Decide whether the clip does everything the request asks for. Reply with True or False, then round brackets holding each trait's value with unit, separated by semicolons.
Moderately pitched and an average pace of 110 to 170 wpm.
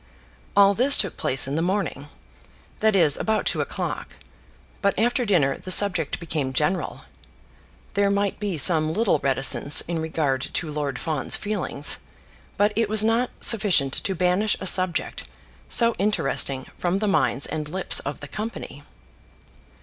True (180 Hz; 150 wpm)